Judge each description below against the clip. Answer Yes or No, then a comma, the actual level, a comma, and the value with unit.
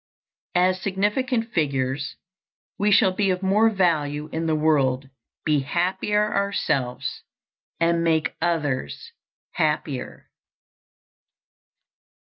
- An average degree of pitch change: Yes, average, 4.9 semitones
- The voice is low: No, medium, 165 Hz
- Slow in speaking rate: Yes, slow, 95 wpm